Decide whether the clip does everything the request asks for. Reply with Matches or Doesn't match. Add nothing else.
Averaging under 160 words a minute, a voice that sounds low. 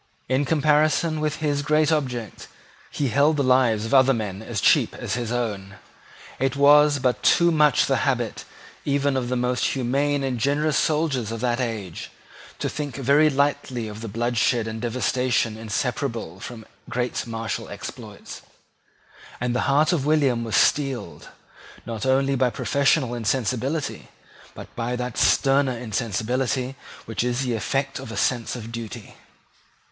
Matches